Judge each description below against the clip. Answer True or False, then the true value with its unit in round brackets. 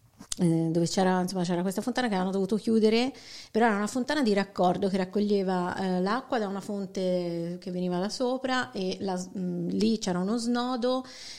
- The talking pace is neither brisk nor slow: False (180 wpm)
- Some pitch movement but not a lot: True (4.2 semitones)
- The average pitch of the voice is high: True (195 Hz)